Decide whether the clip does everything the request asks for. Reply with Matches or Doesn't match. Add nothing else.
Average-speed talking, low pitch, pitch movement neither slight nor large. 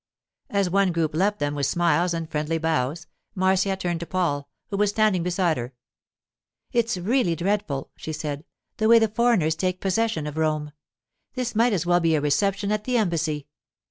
Doesn't match